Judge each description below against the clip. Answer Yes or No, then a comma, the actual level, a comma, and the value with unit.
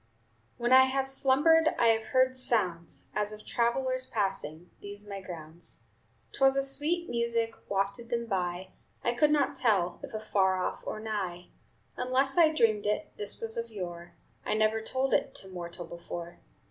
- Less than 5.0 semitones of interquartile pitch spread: No, wide, 5.4 semitones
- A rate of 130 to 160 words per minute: No, average, 170 wpm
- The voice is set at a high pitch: Yes, high, 220 Hz